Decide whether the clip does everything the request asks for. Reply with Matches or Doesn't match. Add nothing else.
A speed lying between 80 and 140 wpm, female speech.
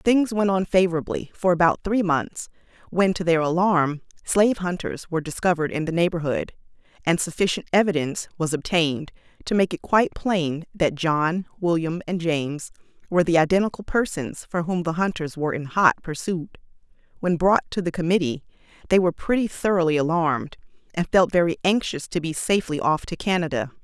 Doesn't match